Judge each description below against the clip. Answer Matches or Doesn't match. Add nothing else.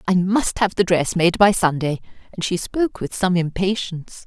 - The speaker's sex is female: Matches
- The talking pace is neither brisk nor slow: Matches